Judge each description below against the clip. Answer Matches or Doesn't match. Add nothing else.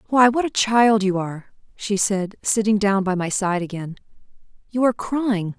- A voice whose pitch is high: Matches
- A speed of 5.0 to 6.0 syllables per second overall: Doesn't match